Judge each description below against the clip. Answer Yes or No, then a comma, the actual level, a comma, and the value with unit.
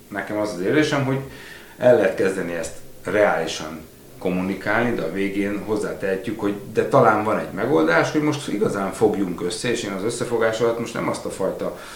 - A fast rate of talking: Yes, fast, 180 wpm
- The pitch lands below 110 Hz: Yes, low, 100 Hz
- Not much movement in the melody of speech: No, average, 3.8 semitones